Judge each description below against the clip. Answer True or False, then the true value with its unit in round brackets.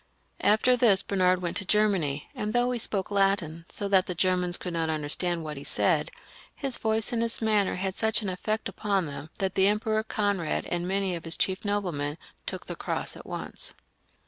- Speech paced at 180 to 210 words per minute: True (200 wpm)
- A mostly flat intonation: False (3.5 semitones)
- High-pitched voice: True (195 Hz)